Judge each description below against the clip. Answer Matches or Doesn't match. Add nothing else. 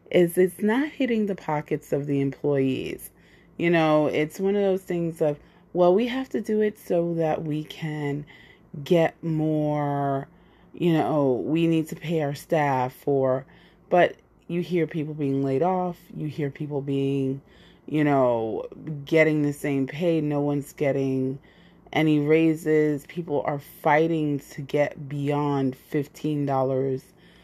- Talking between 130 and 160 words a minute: Matches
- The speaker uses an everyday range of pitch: Matches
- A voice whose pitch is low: Doesn't match